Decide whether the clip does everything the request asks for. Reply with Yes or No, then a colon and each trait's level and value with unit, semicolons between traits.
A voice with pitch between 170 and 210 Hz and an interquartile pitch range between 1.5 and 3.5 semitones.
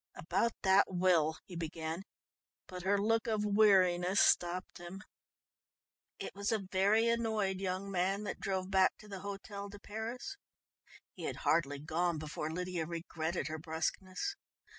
Yes: high, 190 Hz; average, 2.8 semitones